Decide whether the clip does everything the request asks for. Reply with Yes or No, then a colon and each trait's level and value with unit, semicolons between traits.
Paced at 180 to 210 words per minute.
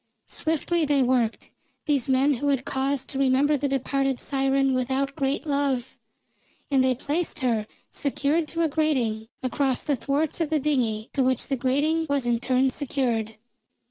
No: average, 165 wpm